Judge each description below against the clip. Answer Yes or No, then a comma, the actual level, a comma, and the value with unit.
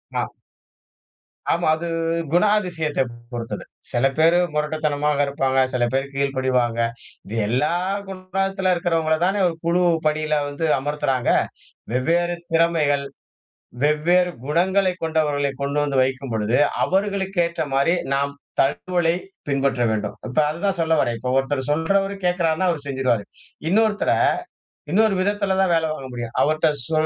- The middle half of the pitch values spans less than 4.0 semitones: No, average, 4.5 semitones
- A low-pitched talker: No, medium, 155 Hz